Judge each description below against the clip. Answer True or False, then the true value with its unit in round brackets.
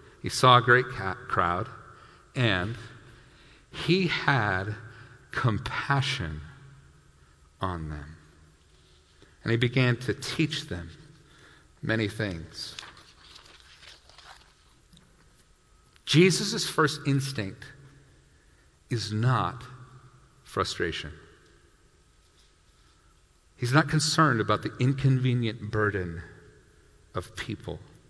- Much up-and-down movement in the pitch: True (8.2 semitones)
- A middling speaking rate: False (75 wpm)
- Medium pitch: False (105 Hz)